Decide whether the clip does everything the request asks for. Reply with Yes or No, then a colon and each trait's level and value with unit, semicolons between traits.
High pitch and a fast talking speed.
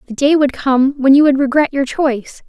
Yes: very high, 275 Hz; fast, 240 wpm